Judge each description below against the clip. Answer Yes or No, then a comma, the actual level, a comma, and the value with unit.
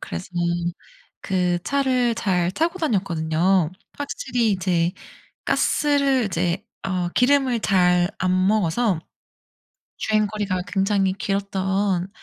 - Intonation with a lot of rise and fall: No, average, 4.2 semitones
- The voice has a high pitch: Yes, high, 195 Hz